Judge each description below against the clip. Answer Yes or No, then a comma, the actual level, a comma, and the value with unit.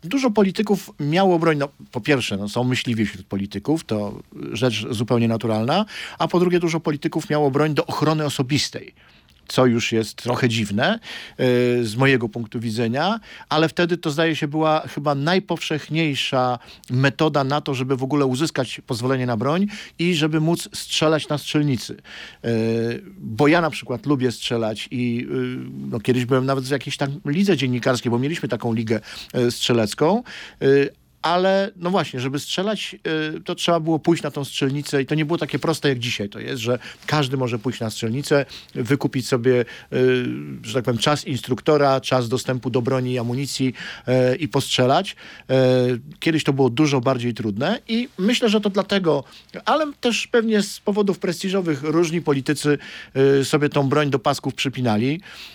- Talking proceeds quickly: Yes, fast, 165 wpm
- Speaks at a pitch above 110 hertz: Yes, medium, 140 Hz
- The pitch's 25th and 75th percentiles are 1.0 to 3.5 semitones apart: No, average, 4.3 semitones